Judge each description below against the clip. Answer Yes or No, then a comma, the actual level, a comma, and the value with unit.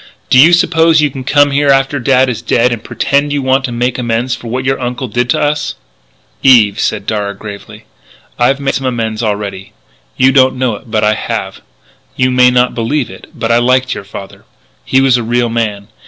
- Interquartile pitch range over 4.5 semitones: No, average, 2.9 semitones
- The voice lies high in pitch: No, low, 125 Hz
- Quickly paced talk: Yes, fast, 210 wpm